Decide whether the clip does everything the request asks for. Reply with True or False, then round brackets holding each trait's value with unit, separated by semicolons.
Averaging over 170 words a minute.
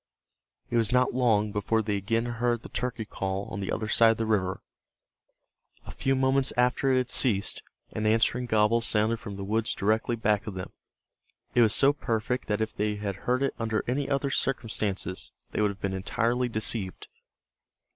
True (185 wpm)